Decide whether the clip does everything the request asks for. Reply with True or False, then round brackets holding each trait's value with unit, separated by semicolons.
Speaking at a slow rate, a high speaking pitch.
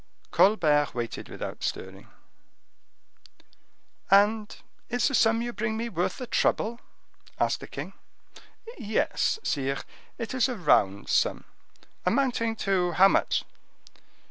True (115 wpm; 210 Hz)